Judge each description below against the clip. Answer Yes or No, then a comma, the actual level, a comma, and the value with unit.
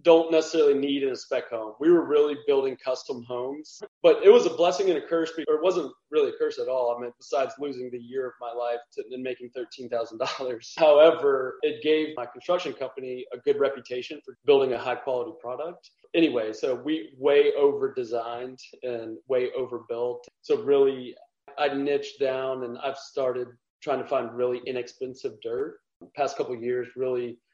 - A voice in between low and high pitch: Yes, medium, 150 Hz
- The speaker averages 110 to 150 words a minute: No, average, 185 wpm